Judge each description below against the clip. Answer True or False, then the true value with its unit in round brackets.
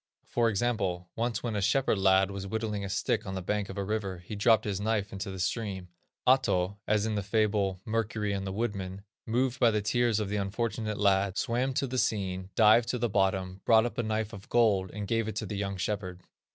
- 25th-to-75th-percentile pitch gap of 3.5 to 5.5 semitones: False (2.7 semitones)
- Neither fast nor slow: False (225 wpm)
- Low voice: True (105 Hz)